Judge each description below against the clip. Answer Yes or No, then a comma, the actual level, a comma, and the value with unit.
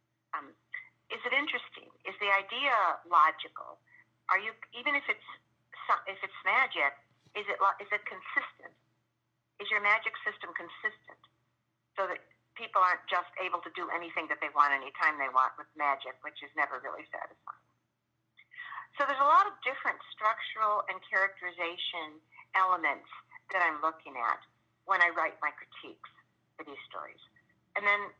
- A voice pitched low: No, high, 195 Hz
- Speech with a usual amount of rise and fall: No, wide, 6.9 semitones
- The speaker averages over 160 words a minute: No, average, 155 wpm